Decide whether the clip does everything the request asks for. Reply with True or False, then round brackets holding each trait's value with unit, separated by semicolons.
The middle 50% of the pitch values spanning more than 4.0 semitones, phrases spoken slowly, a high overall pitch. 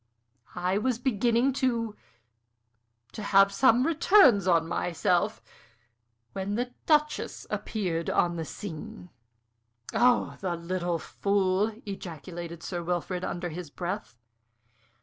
True (4.7 semitones; 110 wpm; 195 Hz)